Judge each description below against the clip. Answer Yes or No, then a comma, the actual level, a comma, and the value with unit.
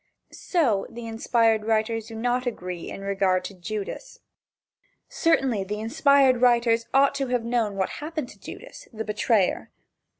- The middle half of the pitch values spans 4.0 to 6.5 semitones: No, average, 3.2 semitones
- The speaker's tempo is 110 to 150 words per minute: Yes, average, 145 wpm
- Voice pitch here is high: Yes, high, 230 Hz